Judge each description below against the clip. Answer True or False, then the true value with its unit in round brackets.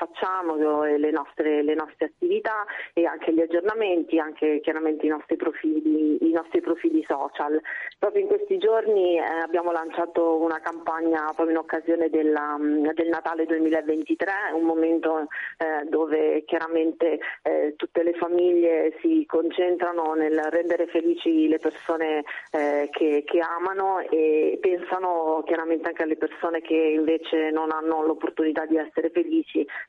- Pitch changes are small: True (1.5 semitones)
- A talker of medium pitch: True (165 Hz)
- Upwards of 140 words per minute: False (130 wpm)